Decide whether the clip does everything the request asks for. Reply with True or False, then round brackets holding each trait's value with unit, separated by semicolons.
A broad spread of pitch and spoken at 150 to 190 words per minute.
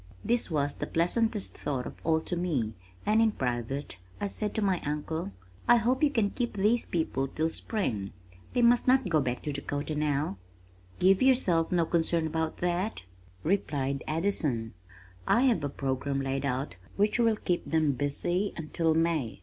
True (6.4 semitones; 170 wpm)